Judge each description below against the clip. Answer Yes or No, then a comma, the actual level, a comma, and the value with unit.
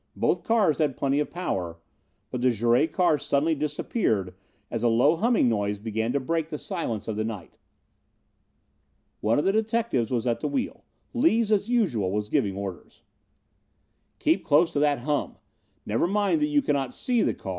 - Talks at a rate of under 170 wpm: No, average, 175 wpm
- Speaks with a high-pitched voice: No, medium, 140 Hz